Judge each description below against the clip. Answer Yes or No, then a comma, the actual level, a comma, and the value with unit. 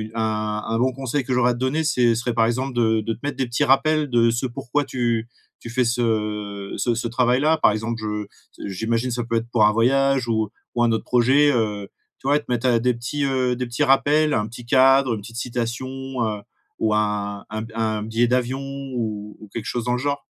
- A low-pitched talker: Yes, low, 120 Hz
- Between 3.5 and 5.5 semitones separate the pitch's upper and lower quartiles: No, average, 2.7 semitones